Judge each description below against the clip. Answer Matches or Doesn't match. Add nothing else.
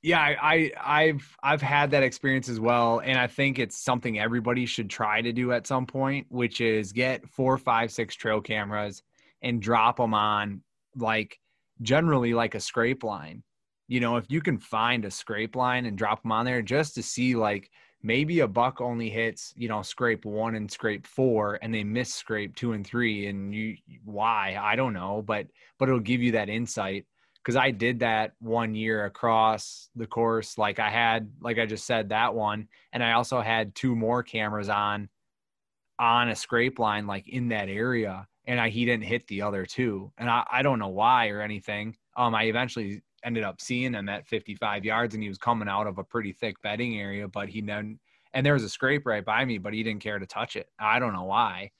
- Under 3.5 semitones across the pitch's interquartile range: Matches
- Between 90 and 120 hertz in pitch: Matches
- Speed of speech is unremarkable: Doesn't match